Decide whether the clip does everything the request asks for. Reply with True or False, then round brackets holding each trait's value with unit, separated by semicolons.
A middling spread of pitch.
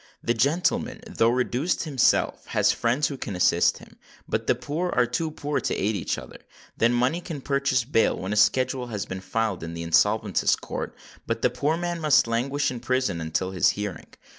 False (5.8 semitones)